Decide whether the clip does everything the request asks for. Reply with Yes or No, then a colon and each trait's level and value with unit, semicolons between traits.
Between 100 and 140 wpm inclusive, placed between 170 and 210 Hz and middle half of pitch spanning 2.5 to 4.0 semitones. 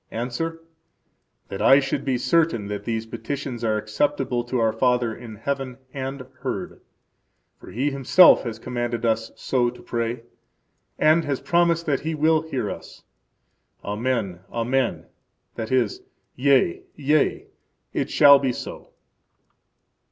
No: slow, 135 wpm; low, 125 Hz; average, 3.6 semitones